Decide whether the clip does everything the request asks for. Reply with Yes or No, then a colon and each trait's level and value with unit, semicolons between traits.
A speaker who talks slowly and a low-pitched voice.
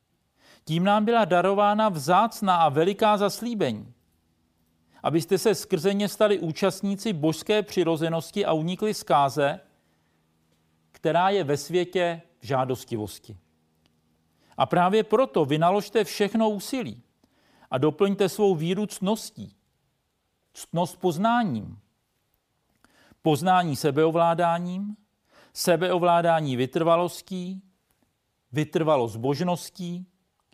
No: slow, 85 wpm; medium, 175 Hz